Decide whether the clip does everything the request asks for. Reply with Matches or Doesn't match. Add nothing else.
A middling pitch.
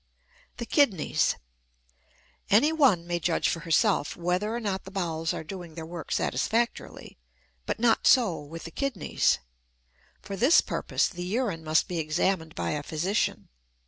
Matches